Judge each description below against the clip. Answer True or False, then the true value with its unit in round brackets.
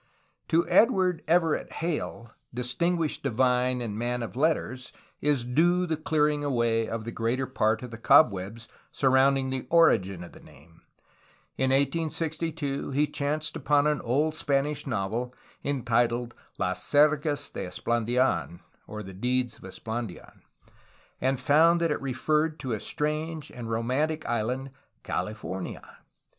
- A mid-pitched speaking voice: False (130 Hz)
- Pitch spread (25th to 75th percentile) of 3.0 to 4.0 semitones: False (4.5 semitones)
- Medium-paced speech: False (130 wpm)